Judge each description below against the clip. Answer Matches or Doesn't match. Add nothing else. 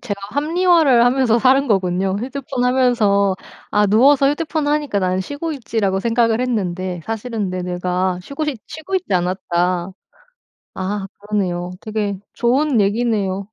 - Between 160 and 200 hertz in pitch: Doesn't match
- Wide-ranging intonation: Matches